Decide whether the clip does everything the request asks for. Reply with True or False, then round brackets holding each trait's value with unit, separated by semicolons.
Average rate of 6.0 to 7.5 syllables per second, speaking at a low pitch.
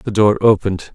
False (5.8 syllables/s; 100 Hz)